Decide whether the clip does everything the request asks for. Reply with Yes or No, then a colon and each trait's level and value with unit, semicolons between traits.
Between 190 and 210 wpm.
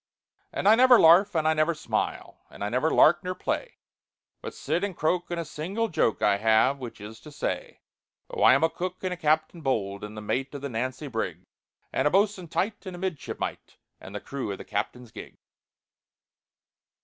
Yes: fast, 205 wpm